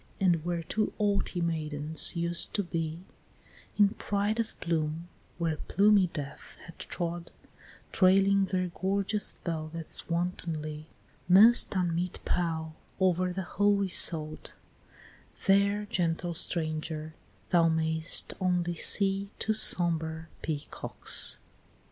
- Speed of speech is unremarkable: No, slow, 105 wpm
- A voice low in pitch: No, medium, 175 Hz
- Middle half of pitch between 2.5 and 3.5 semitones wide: Yes, average, 3.2 semitones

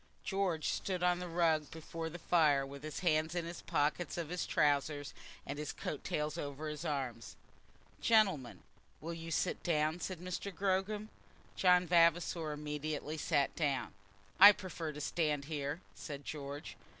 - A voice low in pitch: No, medium, 160 Hz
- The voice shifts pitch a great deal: No, average, 3.0 semitones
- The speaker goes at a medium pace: Yes, average, 160 wpm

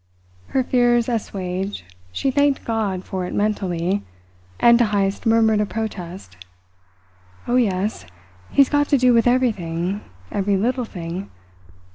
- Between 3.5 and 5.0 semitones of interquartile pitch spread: Yes, average, 4.4 semitones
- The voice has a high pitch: Yes, high, 210 Hz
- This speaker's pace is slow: Yes, slow, 130 wpm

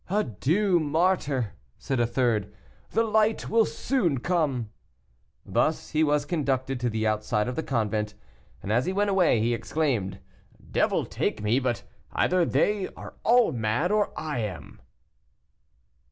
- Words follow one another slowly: No, average, 145 wpm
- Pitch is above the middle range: No, medium, 140 Hz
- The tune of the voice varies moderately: No, wide, 7.9 semitones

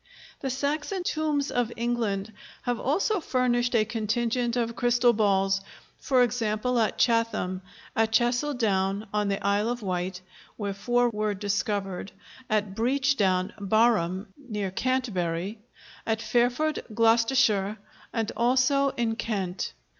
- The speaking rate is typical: No, slow, 125 wpm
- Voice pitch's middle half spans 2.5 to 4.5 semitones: Yes, average, 3.4 semitones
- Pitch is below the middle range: No, high, 225 Hz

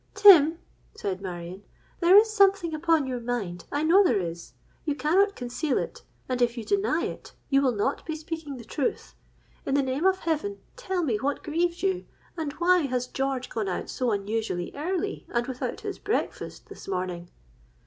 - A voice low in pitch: No, very high, 285 Hz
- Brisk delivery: No, average, 180 wpm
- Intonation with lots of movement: Yes, wide, 6.8 semitones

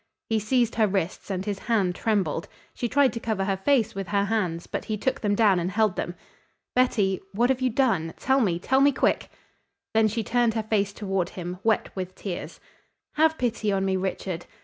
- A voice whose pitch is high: Yes, high, 210 Hz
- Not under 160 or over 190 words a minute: No, fast, 205 wpm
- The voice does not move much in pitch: No, average, 3.5 semitones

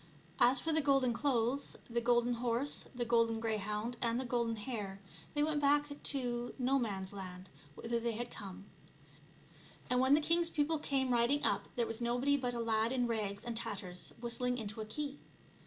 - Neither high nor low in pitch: No, high, 240 Hz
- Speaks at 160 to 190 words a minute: Yes, average, 180 wpm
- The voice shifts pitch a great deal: No, average, 3.0 semitones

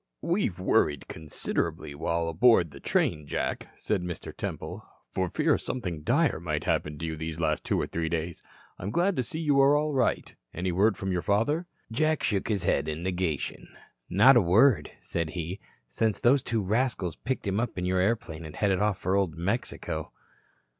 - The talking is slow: No, average, 185 wpm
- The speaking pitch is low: Yes, very low, 95 Hz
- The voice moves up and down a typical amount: No, wide, 6.3 semitones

